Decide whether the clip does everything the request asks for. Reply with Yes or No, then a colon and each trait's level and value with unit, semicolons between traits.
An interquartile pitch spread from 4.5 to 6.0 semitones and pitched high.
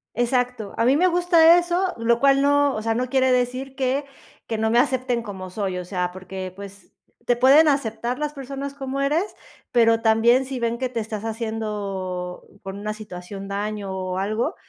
Yes: average, 4.8 semitones; high, 235 Hz